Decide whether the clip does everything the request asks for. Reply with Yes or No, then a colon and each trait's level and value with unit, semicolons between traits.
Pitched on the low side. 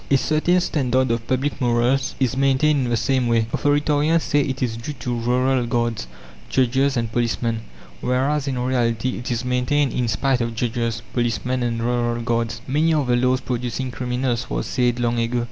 Yes: low, 125 Hz